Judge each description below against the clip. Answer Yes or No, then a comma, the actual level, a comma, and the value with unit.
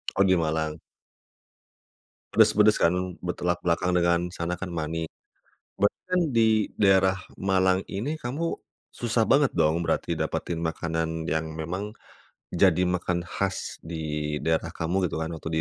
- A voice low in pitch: Yes, very low, 90 Hz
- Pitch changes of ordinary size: Yes, average, 3.1 semitones